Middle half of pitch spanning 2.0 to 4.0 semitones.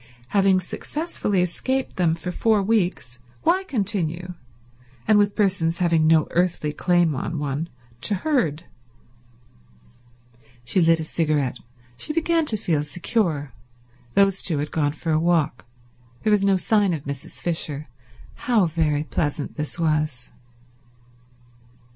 No: average, 4.6 semitones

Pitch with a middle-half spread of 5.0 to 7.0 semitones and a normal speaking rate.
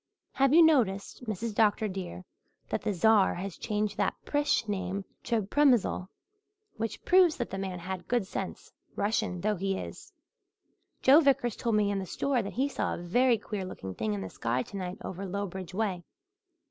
No: average, 4.2 semitones; average, 180 wpm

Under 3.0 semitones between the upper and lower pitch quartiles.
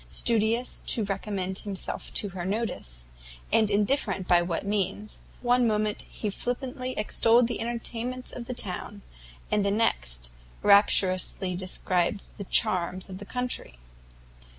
No: average, 3.8 semitones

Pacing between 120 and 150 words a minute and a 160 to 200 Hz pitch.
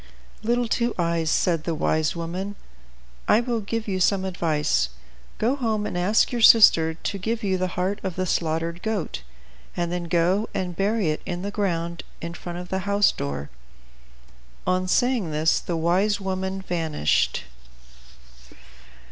No: average, 160 wpm; medium, 185 Hz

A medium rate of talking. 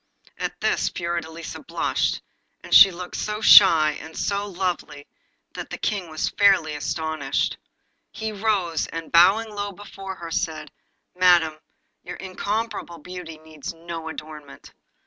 No: slow, 125 wpm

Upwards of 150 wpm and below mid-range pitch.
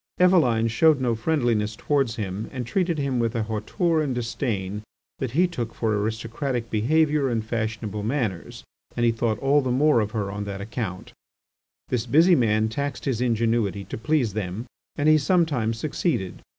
Yes: average, 170 wpm; low, 115 Hz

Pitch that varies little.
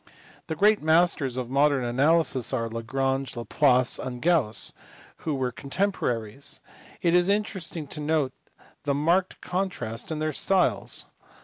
No: average, 5.0 semitones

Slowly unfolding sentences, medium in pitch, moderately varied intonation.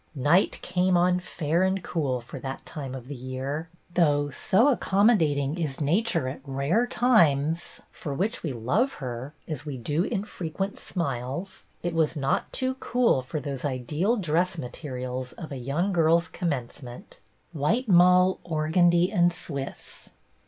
No: average, 155 wpm; medium, 160 Hz; average, 4.8 semitones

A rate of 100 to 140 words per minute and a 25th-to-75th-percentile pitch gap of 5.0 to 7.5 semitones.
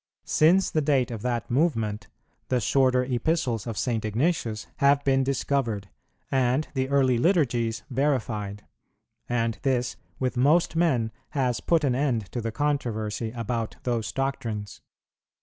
No: slow, 135 wpm; average, 3.5 semitones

